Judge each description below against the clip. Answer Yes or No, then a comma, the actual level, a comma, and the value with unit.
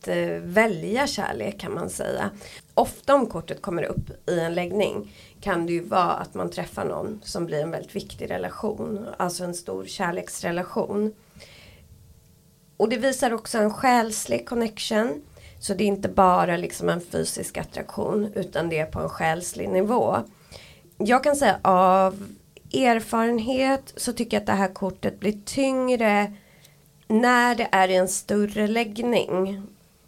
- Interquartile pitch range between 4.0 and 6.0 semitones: Yes, average, 4.5 semitones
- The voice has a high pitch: Yes, high, 200 Hz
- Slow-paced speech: No, average, 150 wpm